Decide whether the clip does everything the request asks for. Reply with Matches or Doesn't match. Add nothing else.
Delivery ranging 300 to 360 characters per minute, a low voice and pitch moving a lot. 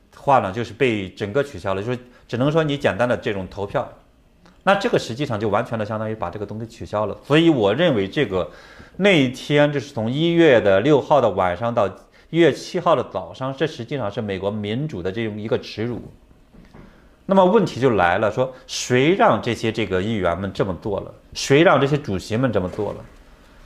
Matches